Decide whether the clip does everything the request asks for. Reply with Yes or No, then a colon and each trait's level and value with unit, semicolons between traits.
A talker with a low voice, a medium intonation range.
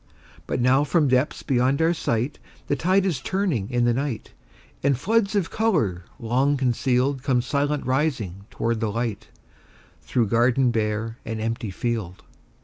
Yes: low, 125 Hz; average, 4.0 semitones